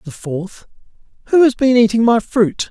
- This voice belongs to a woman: No, male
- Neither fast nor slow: Yes, average, 175 wpm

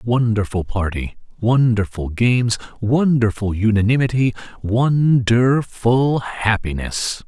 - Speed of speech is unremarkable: No, slow, 80 wpm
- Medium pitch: No, low, 115 Hz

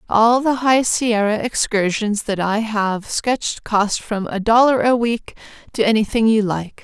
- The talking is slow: No, average, 165 wpm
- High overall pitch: Yes, high, 220 Hz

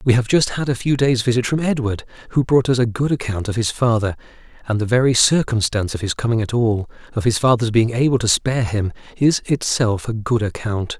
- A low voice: Yes, low, 115 Hz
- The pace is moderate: No, fast, 225 wpm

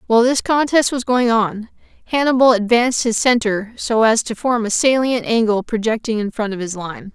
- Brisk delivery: No, average, 195 wpm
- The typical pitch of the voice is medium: No, high, 230 Hz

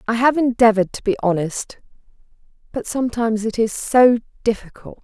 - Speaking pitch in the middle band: No, high, 230 Hz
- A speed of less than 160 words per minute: Yes, average, 145 wpm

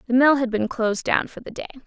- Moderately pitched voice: No, high, 245 Hz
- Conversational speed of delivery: No, fast, 290 wpm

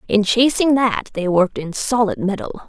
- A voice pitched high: Yes, high, 215 Hz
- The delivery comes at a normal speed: Yes, average, 180 wpm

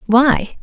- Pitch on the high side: Yes, very high, 255 Hz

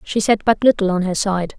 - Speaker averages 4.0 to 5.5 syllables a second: Yes, 5.4 syllables/s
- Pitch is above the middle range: Yes, high, 200 Hz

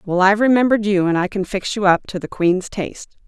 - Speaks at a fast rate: Yes, fast, 255 wpm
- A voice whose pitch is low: No, high, 195 Hz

